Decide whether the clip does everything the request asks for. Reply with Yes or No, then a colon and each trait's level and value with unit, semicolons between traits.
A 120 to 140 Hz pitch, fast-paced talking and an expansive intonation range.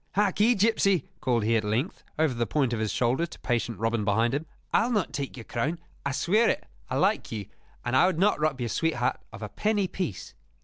Yes: low, 135 Hz; fast, 220 wpm; wide, 7.9 semitones